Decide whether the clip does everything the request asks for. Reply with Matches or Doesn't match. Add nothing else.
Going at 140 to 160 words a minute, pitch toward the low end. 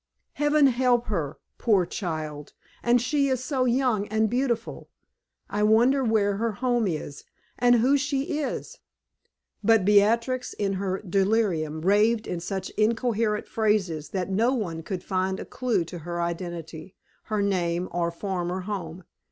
Doesn't match